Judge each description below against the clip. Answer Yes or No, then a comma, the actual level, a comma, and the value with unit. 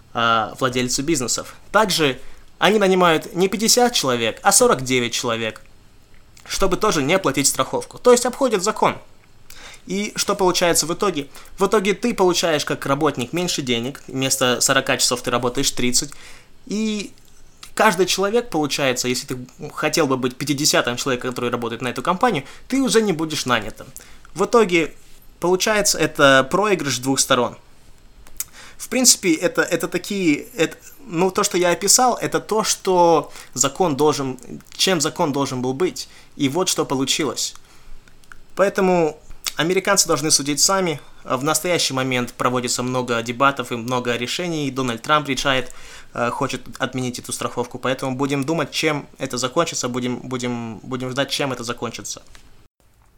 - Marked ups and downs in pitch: Yes, wide, 6.2 semitones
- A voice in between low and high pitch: Yes, medium, 145 Hz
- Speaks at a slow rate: No, average, 140 wpm